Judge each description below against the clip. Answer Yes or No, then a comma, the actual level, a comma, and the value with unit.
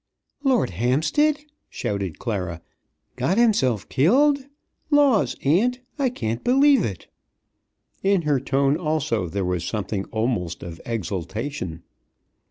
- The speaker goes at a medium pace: No, slow, 110 wpm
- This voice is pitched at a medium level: No, low, 130 Hz